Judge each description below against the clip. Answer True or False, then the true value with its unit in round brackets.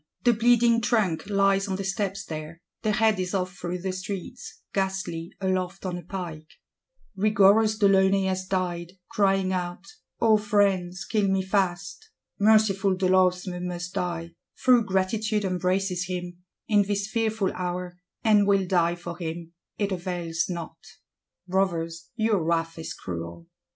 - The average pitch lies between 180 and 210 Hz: True (190 Hz)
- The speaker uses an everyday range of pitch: False (2.3 semitones)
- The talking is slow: False (145 wpm)